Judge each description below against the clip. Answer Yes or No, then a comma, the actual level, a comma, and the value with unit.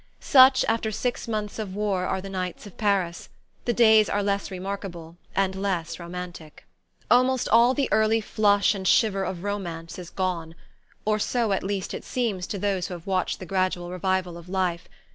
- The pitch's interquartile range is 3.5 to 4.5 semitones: No, average, 3.0 semitones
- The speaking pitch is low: No, high, 195 Hz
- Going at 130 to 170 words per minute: No, average, 180 wpm